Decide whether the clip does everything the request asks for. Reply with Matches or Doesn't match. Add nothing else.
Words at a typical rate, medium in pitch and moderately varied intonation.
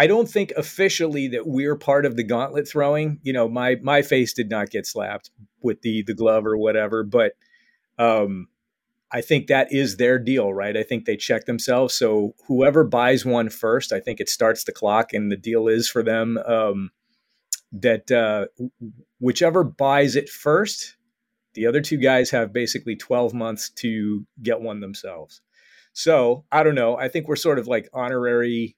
Doesn't match